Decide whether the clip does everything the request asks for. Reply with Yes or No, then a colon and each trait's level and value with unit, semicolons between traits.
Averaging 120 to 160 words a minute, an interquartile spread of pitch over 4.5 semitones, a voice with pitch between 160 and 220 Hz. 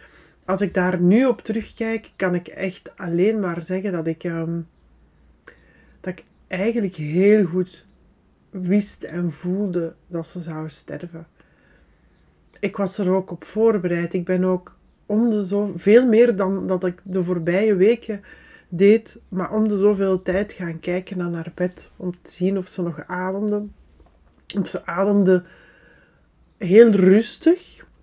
No: average, 150 wpm; average, 2.8 semitones; medium, 185 Hz